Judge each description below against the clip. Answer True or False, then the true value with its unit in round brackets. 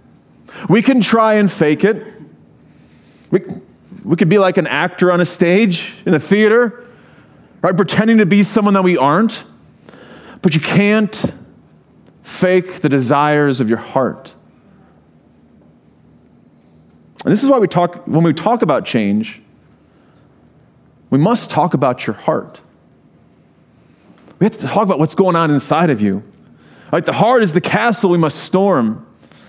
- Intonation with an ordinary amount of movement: False (5.7 semitones)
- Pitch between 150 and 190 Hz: True (185 Hz)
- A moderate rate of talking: True (150 wpm)